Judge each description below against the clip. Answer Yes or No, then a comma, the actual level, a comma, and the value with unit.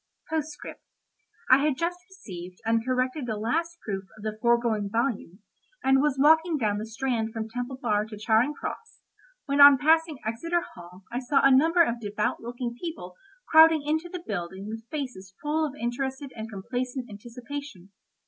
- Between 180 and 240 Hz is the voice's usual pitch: No, very high, 250 Hz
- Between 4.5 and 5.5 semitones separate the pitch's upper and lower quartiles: Yes, average, 5.2 semitones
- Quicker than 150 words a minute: Yes, average, 165 wpm